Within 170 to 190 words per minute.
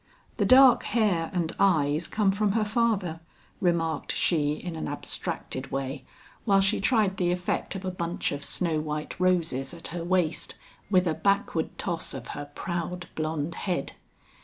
No: average, 160 wpm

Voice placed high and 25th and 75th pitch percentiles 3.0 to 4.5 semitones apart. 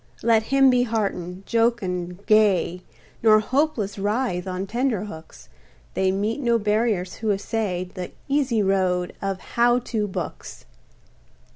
Yes: high, 210 Hz; average, 4.0 semitones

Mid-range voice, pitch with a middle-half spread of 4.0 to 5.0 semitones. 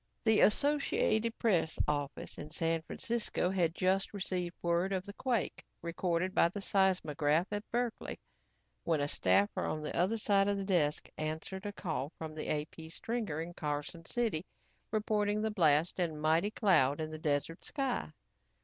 Yes: medium, 180 Hz; average, 4.7 semitones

